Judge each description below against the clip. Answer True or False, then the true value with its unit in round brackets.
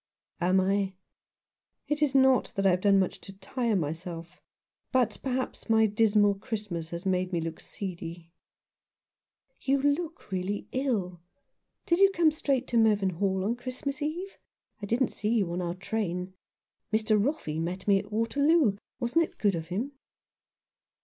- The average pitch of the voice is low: False (205 Hz)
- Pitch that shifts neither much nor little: False (5.9 semitones)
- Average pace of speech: True (160 wpm)